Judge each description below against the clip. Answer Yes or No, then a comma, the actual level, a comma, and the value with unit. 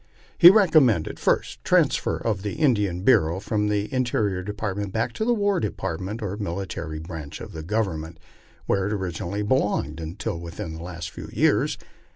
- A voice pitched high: No, low, 100 Hz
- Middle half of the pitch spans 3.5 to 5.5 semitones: Yes, average, 4.6 semitones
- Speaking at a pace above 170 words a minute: Yes, average, 180 wpm